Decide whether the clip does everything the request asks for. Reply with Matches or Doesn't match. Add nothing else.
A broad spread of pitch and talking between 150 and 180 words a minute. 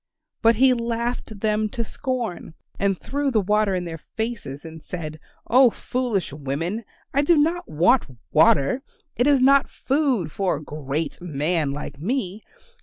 Matches